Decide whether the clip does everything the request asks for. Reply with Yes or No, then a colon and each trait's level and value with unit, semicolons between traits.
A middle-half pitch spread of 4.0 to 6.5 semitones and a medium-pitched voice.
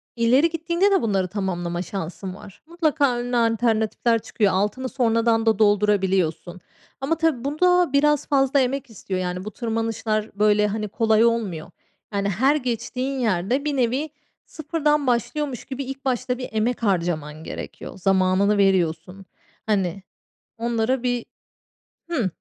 No: average, 5.2 semitones; high, 225 Hz